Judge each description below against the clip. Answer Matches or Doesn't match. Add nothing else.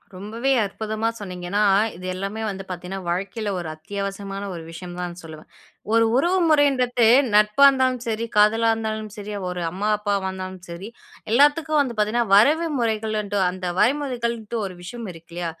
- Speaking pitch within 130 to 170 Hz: Doesn't match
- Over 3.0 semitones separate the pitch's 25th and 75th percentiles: Matches